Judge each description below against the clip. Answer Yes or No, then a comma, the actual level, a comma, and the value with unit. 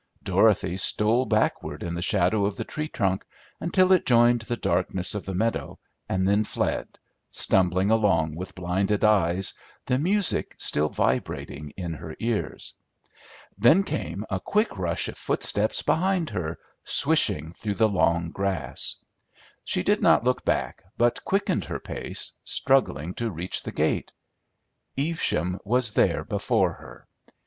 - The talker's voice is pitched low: Yes, low, 100 Hz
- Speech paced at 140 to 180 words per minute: Yes, average, 145 wpm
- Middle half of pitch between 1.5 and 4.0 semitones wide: No, average, 5.1 semitones